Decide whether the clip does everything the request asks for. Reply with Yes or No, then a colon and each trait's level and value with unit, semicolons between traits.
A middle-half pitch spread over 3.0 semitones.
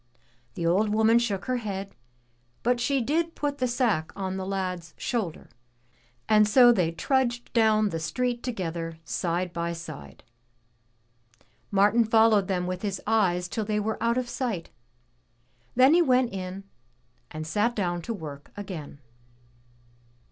Yes: average, 5.0 semitones